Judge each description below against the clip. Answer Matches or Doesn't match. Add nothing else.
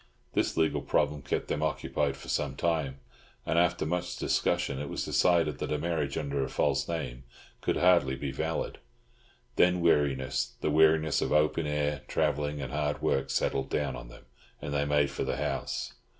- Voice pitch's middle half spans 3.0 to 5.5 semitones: Doesn't match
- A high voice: Doesn't match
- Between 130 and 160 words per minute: Doesn't match